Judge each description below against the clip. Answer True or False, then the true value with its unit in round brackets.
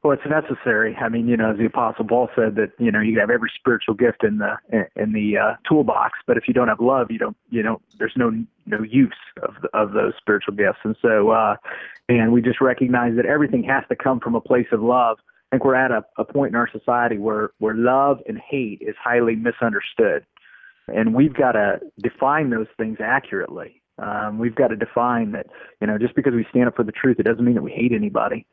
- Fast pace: True (235 wpm)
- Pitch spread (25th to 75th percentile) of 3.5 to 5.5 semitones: False (3.0 semitones)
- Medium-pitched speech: False (120 Hz)